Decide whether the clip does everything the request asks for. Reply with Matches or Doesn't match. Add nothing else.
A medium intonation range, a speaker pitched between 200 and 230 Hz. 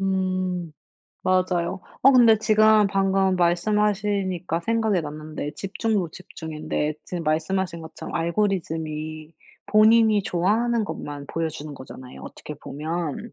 Doesn't match